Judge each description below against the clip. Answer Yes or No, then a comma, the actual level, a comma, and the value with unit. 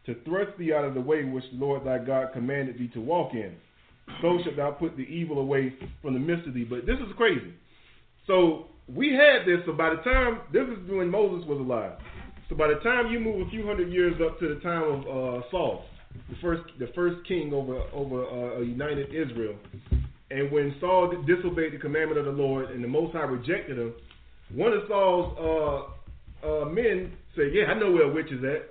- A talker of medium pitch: Yes, medium, 155 Hz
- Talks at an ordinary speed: No, fast, 220 wpm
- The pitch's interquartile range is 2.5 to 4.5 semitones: No, wide, 5.4 semitones